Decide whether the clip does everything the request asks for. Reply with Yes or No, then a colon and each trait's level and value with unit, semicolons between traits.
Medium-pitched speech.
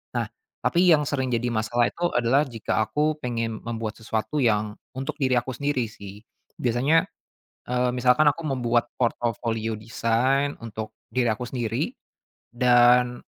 No: low, 120 Hz